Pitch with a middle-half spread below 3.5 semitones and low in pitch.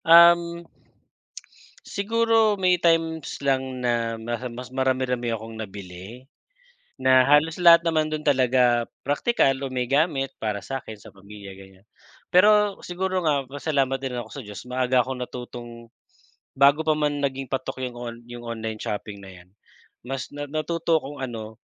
No: average, 4.9 semitones; low, 130 Hz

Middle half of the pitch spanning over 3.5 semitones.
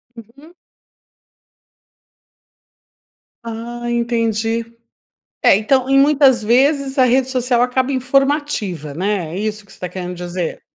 Yes: average, 4.2 semitones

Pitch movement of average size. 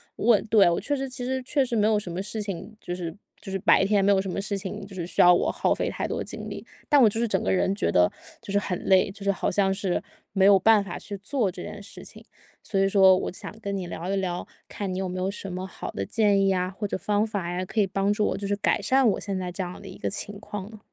No: narrow, 2.0 semitones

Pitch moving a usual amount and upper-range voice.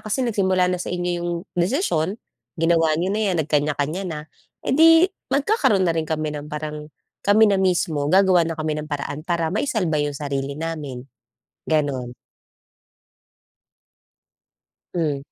No: average, 4.0 semitones; medium, 165 Hz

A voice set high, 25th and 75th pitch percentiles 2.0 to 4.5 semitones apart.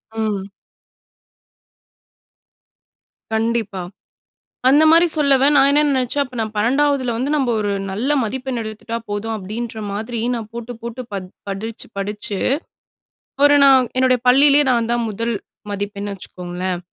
Yes: high, 230 Hz; average, 4.1 semitones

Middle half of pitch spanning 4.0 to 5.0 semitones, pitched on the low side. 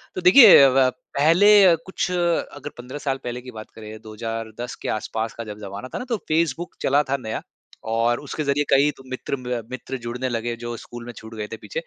Yes: average, 4.5 semitones; low, 125 Hz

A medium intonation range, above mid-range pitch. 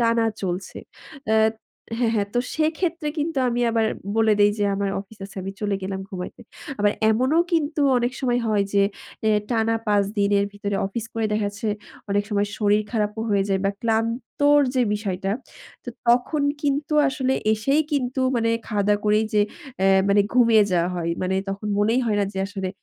Yes: average, 3.2 semitones; high, 215 Hz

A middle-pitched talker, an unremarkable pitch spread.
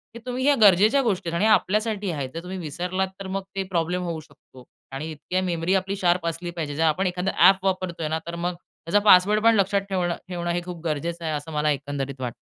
Yes: medium, 175 Hz; average, 3.0 semitones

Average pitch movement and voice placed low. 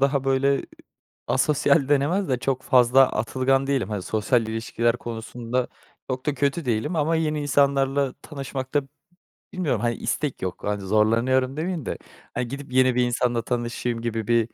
Yes: average, 3.0 semitones; low, 130 Hz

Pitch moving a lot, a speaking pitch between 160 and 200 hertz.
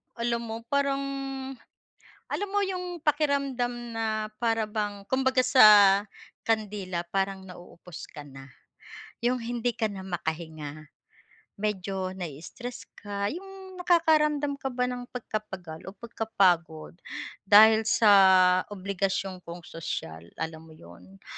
No: wide, 5.9 semitones; high, 215 Hz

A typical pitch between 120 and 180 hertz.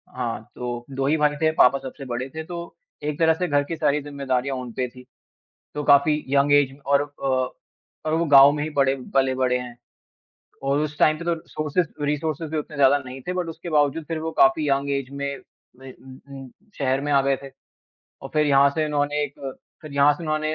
Yes: medium, 140 Hz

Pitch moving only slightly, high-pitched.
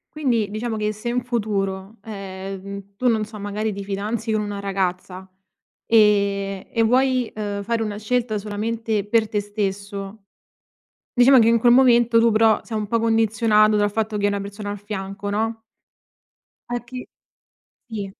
Yes: narrow, 2.2 semitones; high, 215 Hz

